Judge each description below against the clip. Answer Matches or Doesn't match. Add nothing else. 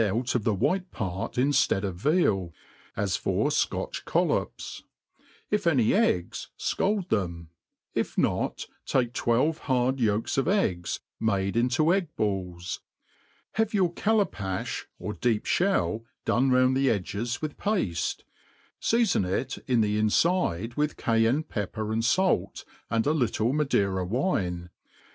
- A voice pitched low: Matches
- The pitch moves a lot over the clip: Matches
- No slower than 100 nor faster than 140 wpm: Matches